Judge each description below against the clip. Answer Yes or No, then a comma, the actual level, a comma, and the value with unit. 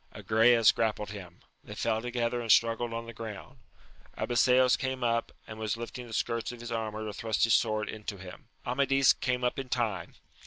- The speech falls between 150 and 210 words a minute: Yes, average, 190 wpm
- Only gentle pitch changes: Yes, narrow, 2.1 semitones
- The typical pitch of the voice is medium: No, low, 115 Hz